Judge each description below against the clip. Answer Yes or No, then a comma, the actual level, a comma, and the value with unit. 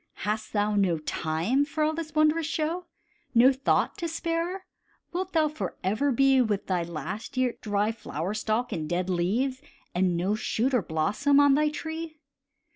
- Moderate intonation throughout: No, wide, 7.9 semitones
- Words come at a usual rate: Yes, average, 170 wpm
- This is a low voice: No, very high, 250 Hz